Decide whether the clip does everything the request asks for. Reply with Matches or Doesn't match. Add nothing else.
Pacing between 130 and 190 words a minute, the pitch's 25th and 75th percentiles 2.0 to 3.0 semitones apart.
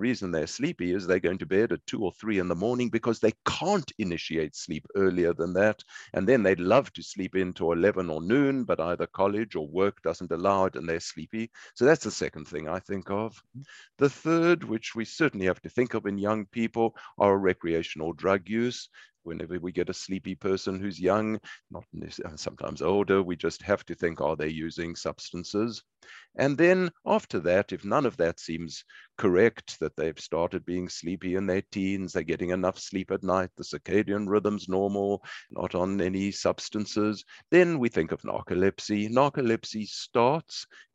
Doesn't match